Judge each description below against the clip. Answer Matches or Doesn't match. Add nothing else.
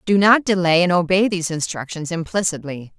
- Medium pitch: Matches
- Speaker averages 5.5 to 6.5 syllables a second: Matches